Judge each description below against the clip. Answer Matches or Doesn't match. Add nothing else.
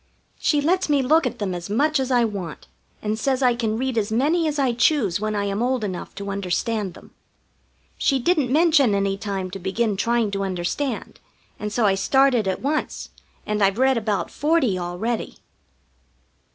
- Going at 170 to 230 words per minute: Matches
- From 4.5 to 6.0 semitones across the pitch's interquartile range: Matches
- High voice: Matches